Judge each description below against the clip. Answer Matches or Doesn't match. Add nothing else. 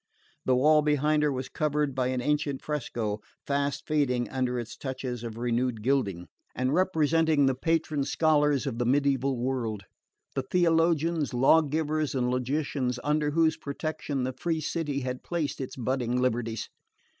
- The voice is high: Doesn't match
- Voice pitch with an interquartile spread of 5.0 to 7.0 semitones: Doesn't match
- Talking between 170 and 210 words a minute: Doesn't match